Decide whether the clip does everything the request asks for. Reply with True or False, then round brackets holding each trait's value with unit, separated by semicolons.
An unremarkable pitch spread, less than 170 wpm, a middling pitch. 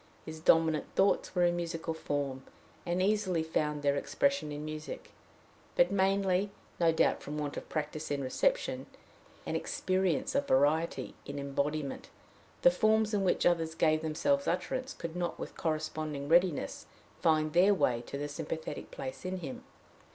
True (3.7 semitones; 155 wpm; 160 Hz)